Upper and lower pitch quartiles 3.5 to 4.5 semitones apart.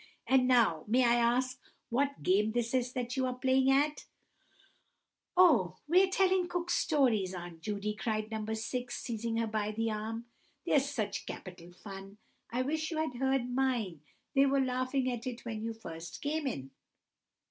Yes: average, 3.9 semitones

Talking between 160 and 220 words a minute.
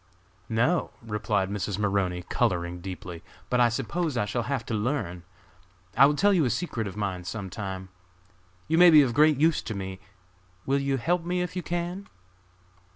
Yes: average, 180 wpm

